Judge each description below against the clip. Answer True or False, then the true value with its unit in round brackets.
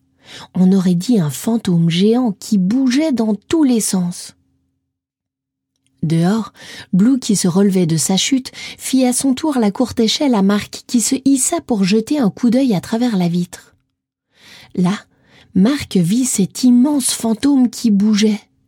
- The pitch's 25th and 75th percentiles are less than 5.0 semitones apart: False (5.4 semitones)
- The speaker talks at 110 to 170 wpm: True (155 wpm)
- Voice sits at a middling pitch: False (215 Hz)